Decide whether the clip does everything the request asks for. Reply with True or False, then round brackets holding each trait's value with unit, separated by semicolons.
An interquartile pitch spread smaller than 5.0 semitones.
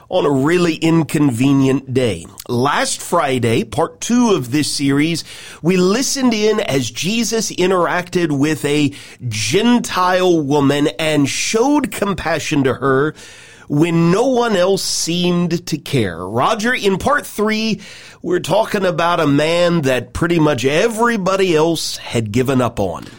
False (5.5 semitones)